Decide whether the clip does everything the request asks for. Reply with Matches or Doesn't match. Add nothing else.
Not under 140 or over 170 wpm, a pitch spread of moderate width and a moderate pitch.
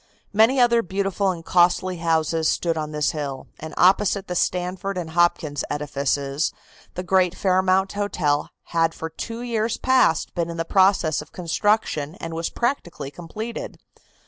Matches